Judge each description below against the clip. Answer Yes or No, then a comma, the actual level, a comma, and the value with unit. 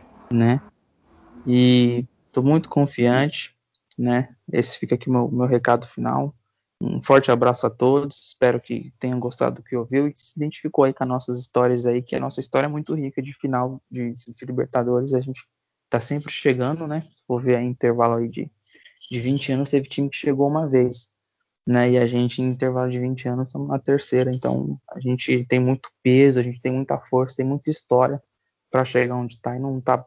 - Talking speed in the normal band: No, fast, 200 wpm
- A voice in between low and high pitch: No, low, 125 Hz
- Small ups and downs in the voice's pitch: Yes, narrow, 1.9 semitones